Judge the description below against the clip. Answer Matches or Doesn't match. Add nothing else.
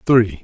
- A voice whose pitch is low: Matches